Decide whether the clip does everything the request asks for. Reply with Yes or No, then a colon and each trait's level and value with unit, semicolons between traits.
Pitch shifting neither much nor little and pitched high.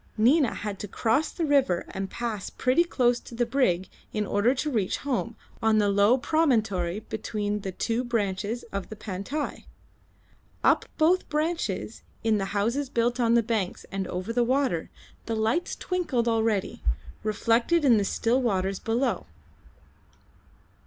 Yes: average, 4.1 semitones; high, 230 Hz